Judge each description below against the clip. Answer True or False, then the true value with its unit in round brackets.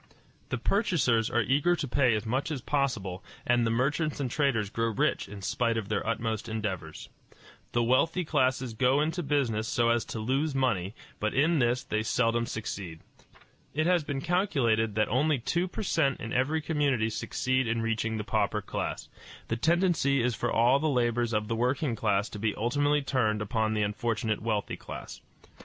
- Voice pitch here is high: False (120 Hz)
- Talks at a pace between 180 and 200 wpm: True (185 wpm)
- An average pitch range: True (4.3 semitones)